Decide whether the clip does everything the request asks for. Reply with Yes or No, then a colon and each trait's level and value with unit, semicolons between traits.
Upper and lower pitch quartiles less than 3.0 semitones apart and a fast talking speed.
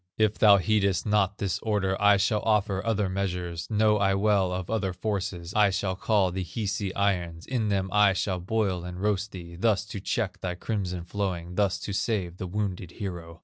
No: narrow, 2.5 semitones; average, 190 wpm